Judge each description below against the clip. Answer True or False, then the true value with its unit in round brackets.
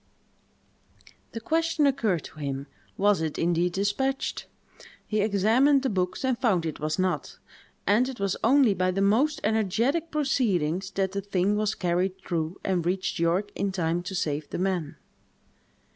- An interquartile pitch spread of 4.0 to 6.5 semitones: True (4.5 semitones)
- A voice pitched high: True (195 Hz)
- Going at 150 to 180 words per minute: True (160 wpm)